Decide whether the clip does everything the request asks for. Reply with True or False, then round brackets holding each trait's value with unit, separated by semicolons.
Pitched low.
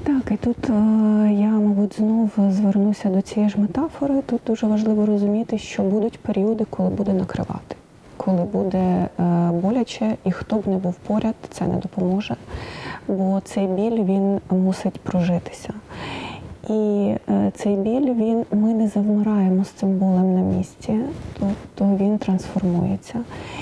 False (205 Hz)